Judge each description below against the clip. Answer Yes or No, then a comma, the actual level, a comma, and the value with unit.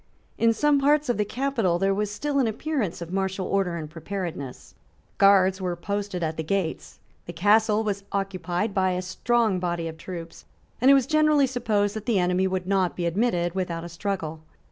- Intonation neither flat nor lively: Yes, average, 4.0 semitones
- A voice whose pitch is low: No, high, 195 Hz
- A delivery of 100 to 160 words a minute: No, average, 190 wpm